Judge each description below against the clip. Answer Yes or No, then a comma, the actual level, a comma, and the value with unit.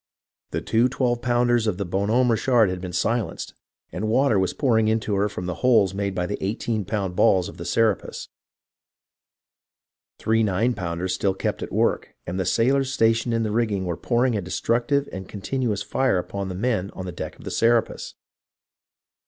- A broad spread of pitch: No, average, 4.1 semitones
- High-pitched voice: No, low, 110 Hz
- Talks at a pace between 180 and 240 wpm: Yes, average, 185 wpm